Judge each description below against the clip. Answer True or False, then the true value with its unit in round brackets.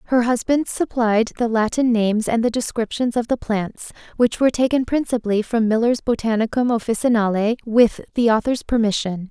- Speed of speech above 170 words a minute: False (155 wpm)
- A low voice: False (230 Hz)